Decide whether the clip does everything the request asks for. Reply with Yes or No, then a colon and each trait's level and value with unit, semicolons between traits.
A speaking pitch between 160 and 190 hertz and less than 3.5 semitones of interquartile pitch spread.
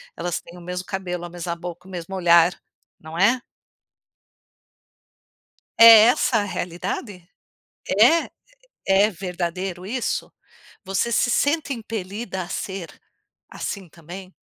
Yes: medium, 185 Hz; average, 2.8 semitones